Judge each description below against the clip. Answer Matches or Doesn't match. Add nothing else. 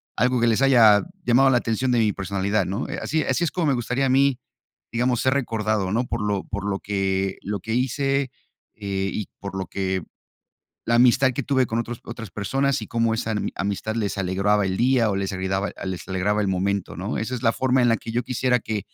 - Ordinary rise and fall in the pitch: Matches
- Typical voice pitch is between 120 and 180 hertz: Doesn't match